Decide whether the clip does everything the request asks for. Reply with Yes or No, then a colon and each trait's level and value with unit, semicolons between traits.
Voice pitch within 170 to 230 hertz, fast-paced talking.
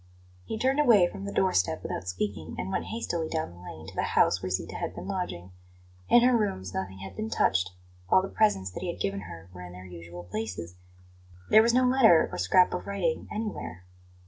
No: low, 110 Hz; fast, 220 wpm